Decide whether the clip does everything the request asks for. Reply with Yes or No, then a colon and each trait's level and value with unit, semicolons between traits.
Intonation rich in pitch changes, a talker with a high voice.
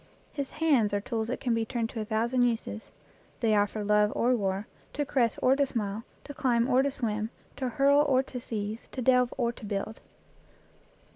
No: average, 3.3 semitones; high, 235 Hz